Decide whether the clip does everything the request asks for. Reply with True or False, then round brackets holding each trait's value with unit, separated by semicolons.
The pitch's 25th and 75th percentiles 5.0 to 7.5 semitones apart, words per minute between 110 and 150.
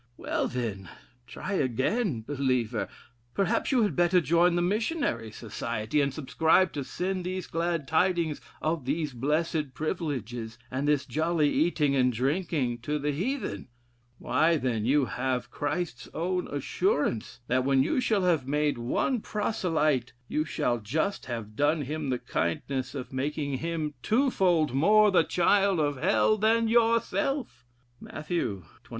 True (5.6 semitones; 145 wpm)